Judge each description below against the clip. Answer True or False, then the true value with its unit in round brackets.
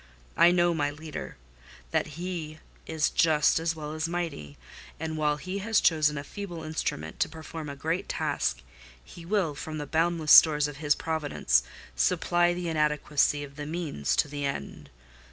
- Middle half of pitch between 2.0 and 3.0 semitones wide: True (2.4 semitones)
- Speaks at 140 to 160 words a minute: False (170 wpm)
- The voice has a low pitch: False (155 Hz)